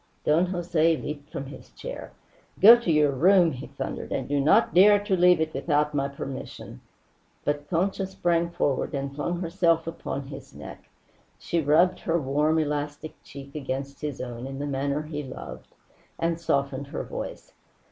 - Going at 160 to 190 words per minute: Yes, average, 170 wpm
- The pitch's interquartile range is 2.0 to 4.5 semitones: Yes, average, 3.5 semitones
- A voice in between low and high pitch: Yes, medium, 150 Hz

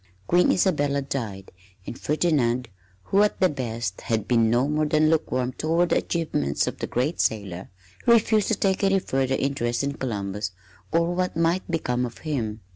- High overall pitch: No, medium, 140 Hz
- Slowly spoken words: No, average, 170 wpm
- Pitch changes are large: Yes, wide, 6.2 semitones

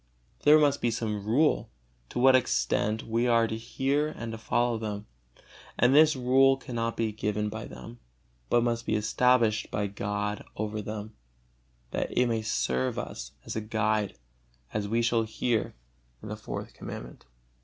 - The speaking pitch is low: Yes, low, 115 Hz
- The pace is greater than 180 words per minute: No, average, 165 wpm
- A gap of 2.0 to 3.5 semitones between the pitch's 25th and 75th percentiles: Yes, narrow, 2.5 semitones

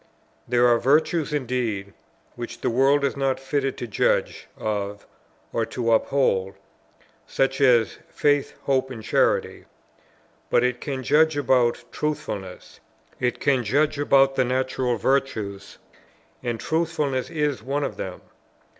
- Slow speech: Yes, slow, 130 wpm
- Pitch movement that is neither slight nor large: Yes, average, 3.0 semitones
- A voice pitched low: Yes, low, 130 Hz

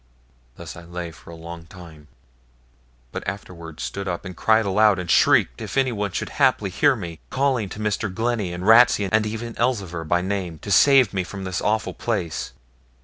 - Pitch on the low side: Yes, low, 100 Hz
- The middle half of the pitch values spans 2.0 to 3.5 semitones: No, average, 4.2 semitones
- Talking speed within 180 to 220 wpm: Yes, average, 185 wpm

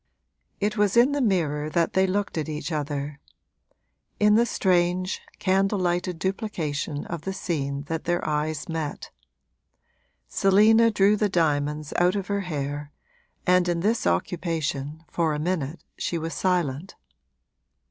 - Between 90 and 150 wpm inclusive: Yes, average, 140 wpm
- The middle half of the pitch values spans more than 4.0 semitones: Yes, average, 4.4 semitones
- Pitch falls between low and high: Yes, medium, 175 Hz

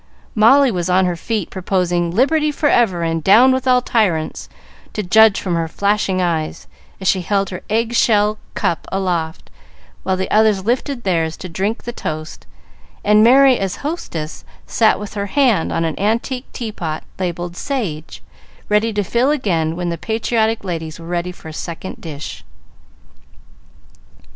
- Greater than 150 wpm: Yes, average, 160 wpm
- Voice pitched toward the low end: No, high, 195 Hz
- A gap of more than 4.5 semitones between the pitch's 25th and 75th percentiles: Yes, average, 4.9 semitones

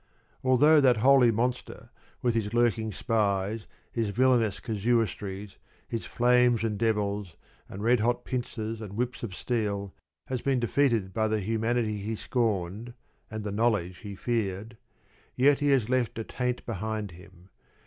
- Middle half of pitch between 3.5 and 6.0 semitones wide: No, average, 3.0 semitones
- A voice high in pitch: No, low, 115 Hz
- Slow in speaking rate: No, average, 150 wpm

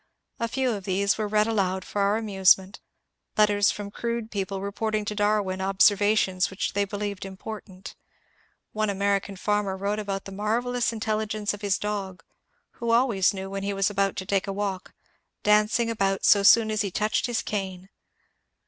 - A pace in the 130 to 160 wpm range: No, average, 170 wpm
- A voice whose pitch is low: No, high, 205 Hz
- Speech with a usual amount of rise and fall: No, narrow, 1.6 semitones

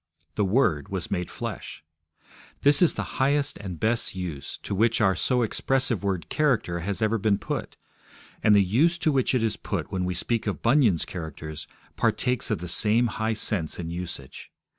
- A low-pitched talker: Yes, low, 105 Hz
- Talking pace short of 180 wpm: No, average, 185 wpm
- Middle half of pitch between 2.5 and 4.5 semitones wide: No, average, 5.2 semitones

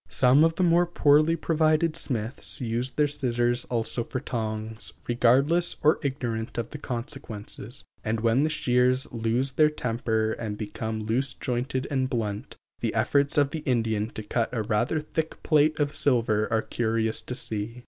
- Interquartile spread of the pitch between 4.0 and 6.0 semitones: Yes, average, 4.4 semitones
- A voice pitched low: Yes, low, 125 Hz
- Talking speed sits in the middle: Yes, average, 160 wpm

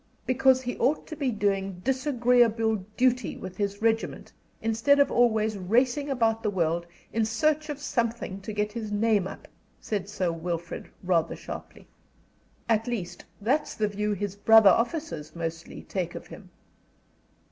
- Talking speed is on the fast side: No, average, 150 wpm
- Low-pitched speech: No, high, 220 Hz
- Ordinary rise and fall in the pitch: Yes, average, 4.0 semitones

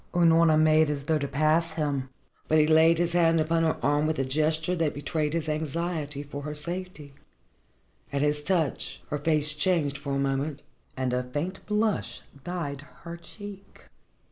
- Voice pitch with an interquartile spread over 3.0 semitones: No, narrow, 2.5 semitones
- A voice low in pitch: No, medium, 155 Hz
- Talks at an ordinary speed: Yes, average, 175 wpm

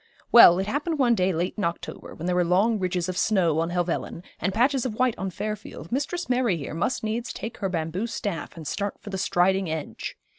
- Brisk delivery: Yes, fast, 220 wpm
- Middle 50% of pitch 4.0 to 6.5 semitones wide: Yes, average, 4.8 semitones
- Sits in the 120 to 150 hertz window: No, high, 190 Hz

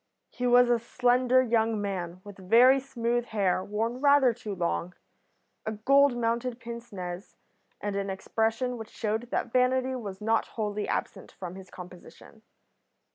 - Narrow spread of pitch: No, average, 3.6 semitones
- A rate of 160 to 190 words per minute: No, average, 150 wpm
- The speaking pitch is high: Yes, high, 225 Hz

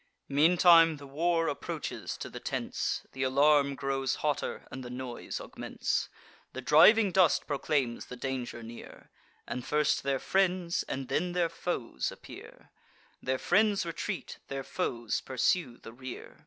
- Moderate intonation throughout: Yes, average, 4.6 semitones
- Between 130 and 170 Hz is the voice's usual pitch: Yes, medium, 140 Hz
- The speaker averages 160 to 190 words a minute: No, average, 140 wpm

